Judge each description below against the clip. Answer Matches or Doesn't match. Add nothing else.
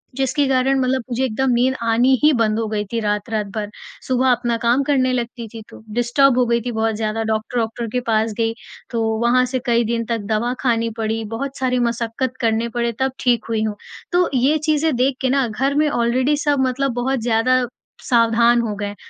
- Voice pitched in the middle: Doesn't match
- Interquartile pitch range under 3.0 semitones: Matches